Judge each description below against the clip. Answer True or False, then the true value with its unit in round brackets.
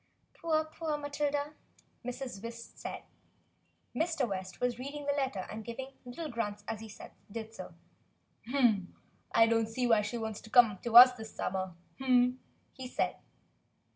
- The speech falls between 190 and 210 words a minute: False (150 wpm)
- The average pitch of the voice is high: True (240 Hz)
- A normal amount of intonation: True (3.8 semitones)